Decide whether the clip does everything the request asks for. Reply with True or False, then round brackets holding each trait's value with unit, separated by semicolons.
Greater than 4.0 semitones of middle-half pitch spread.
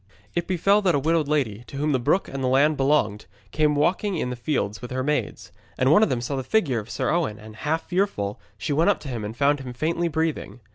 True (4.9 semitones)